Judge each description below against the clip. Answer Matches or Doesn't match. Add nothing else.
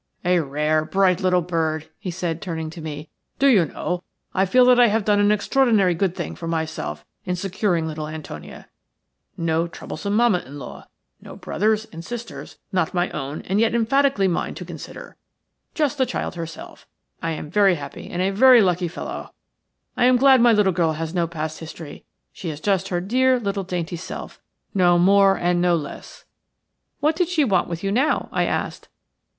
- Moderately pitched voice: Matches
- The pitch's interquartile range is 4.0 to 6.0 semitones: Matches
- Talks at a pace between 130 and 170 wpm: Doesn't match